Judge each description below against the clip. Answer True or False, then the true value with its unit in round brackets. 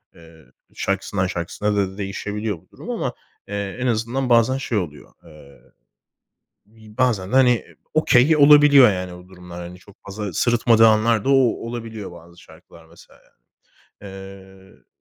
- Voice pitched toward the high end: False (105 Hz)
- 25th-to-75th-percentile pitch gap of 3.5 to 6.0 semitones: True (4.3 semitones)